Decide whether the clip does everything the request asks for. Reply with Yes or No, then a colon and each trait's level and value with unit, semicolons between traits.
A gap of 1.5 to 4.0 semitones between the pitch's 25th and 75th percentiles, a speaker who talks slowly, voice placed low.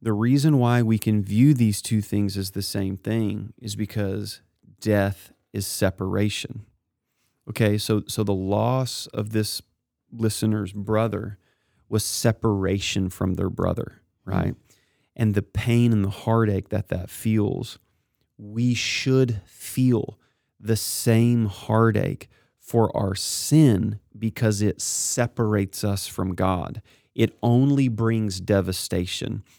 Yes: narrow, 2.5 semitones; slow, 125 wpm; low, 110 Hz